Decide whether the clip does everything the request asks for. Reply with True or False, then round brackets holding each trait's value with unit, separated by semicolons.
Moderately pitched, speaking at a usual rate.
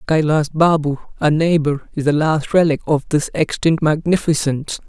True (155 Hz; 150 wpm)